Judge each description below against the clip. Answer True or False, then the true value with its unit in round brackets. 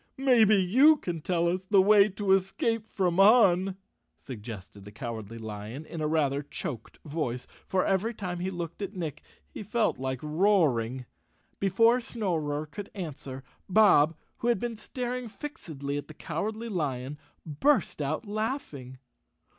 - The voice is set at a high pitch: False (175 Hz)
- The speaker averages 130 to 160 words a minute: True (150 wpm)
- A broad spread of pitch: True (6.8 semitones)